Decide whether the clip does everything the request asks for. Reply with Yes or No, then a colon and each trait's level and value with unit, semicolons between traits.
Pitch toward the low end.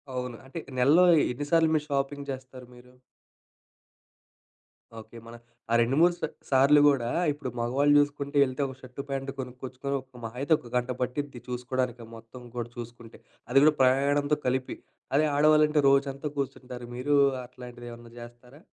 Yes: low, 130 Hz